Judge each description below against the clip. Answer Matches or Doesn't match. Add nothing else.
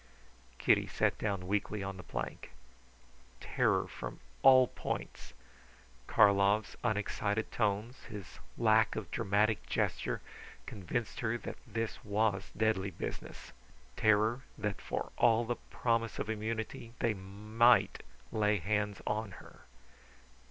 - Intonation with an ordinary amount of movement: Doesn't match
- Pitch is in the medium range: Doesn't match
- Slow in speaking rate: Matches